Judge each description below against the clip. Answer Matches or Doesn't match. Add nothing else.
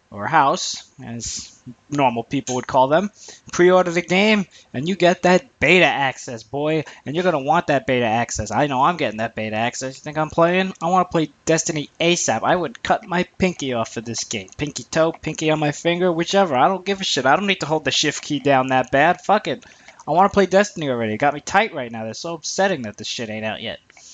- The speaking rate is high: Matches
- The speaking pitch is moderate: Matches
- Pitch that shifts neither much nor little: Doesn't match